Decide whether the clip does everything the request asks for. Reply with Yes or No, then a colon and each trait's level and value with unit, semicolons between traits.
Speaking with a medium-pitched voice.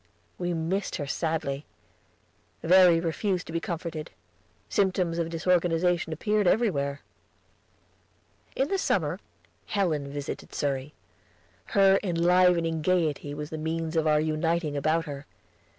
Yes: medium, 165 Hz